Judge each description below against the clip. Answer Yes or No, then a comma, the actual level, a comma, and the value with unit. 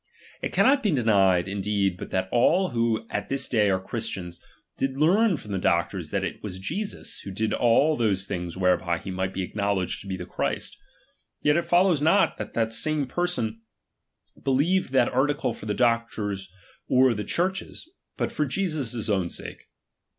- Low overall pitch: Yes, low, 115 Hz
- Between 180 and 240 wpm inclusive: Yes, average, 190 wpm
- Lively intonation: Yes, wide, 7.1 semitones